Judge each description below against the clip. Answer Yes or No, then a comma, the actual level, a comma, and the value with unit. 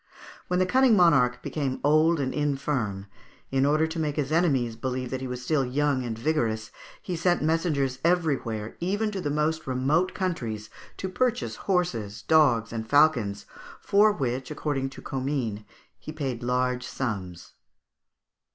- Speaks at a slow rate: No, average, 155 wpm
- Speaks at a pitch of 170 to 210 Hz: No, medium, 140 Hz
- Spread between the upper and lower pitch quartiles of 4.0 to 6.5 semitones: Yes, average, 4.5 semitones